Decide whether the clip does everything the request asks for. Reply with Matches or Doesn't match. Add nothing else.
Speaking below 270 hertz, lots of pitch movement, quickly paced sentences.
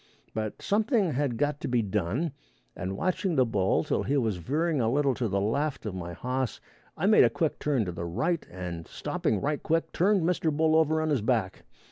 Matches